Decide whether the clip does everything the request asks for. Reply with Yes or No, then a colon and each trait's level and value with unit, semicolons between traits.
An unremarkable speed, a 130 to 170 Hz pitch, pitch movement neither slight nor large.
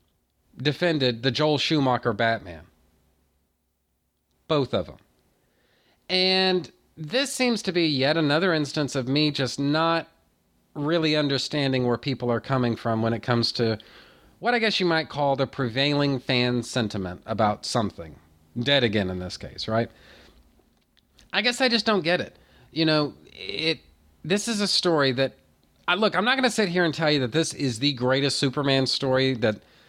No: average, 165 wpm; low, 135 Hz; wide, 6.2 semitones